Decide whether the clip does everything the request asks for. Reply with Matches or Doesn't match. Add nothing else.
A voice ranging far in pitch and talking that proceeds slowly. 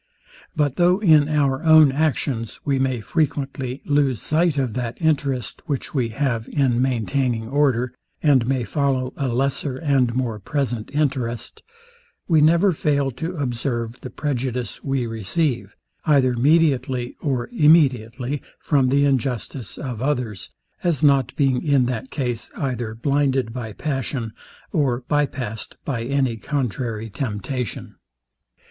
Doesn't match